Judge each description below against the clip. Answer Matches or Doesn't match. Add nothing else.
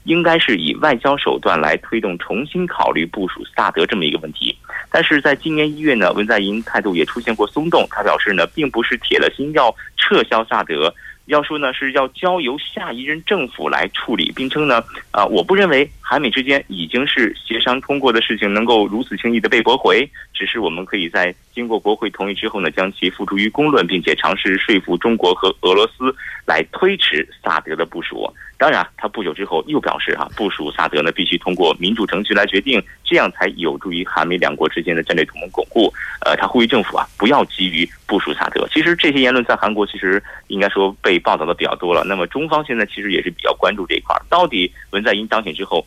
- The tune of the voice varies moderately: Doesn't match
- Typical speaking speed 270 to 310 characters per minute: Doesn't match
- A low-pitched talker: Matches